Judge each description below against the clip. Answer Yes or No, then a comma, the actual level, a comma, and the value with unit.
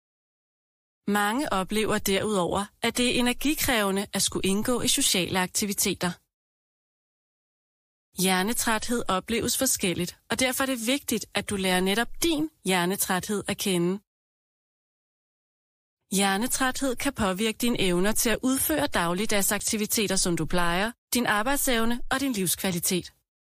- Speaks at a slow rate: Yes, slow, 115 wpm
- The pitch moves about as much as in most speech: Yes, average, 4.6 semitones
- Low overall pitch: No, high, 210 Hz